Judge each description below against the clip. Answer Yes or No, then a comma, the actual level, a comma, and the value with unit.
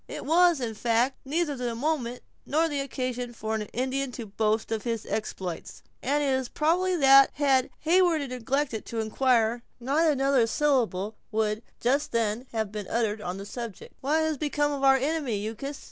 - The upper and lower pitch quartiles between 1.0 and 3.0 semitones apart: No, average, 4.4 semitones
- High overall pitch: Yes, very high, 255 Hz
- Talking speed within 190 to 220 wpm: No, average, 175 wpm